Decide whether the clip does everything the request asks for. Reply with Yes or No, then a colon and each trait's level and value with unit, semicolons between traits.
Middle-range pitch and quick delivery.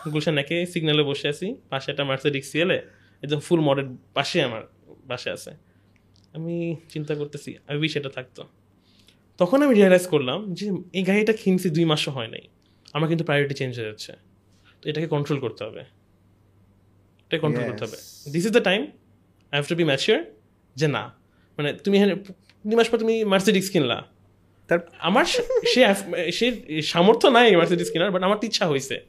Yes: medium, 155 Hz; fast, 165 wpm